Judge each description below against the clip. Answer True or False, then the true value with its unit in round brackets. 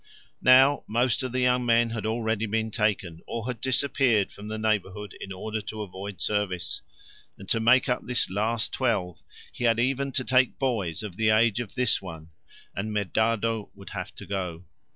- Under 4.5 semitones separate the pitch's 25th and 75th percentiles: True (3.3 semitones)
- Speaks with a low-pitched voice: True (110 Hz)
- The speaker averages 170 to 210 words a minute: True (185 wpm)